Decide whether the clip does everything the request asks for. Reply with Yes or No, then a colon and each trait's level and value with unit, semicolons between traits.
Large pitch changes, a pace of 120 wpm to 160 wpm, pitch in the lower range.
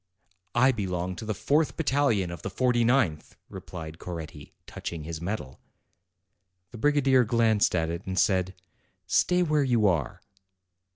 Yes: wide, 6.9 semitones; average, 140 wpm; low, 105 Hz